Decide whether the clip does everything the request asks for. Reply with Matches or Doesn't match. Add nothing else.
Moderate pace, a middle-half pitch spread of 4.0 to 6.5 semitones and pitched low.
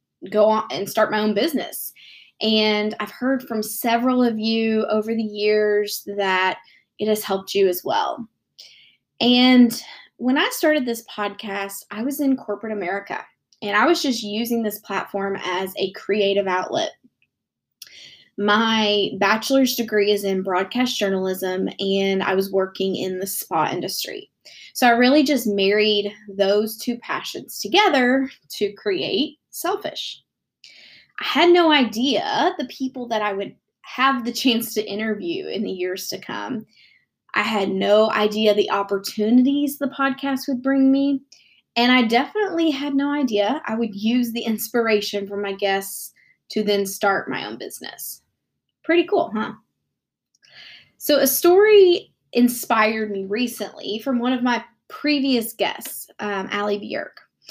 Doesn't match